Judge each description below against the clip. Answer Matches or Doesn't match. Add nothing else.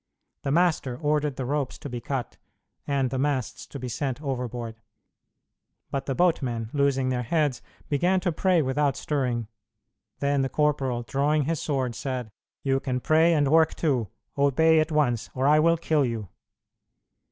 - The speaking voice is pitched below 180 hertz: Matches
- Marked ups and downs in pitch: Doesn't match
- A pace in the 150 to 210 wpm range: Matches